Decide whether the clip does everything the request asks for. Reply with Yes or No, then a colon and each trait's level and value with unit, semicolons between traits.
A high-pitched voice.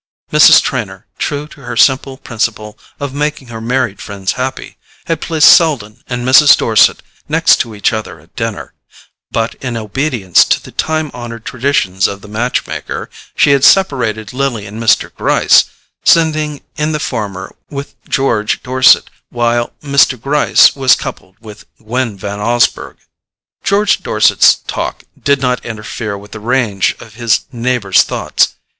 No: low, 120 Hz